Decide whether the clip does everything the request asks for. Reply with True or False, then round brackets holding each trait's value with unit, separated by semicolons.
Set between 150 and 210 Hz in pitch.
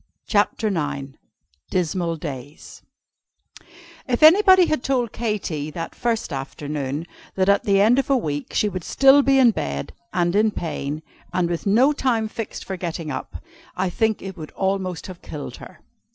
True (190 Hz)